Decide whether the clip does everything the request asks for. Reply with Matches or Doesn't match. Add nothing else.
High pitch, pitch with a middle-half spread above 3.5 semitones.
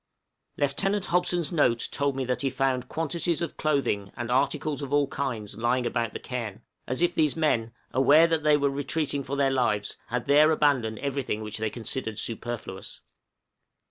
Doesn't match